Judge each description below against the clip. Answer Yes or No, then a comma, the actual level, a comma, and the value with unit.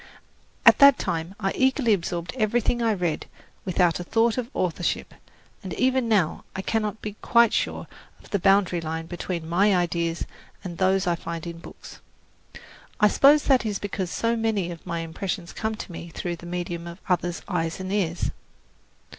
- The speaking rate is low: No, average, 175 wpm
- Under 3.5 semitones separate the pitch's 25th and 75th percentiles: No, average, 4.1 semitones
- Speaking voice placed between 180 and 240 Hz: Yes, medium, 185 Hz